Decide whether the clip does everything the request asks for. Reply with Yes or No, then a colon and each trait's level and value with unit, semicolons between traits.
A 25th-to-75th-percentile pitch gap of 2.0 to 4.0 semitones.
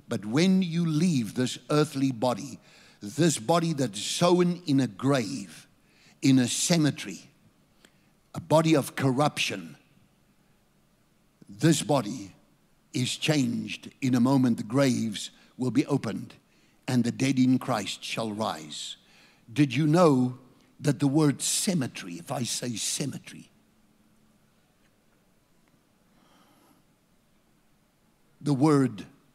Yes: average, 3.5 semitones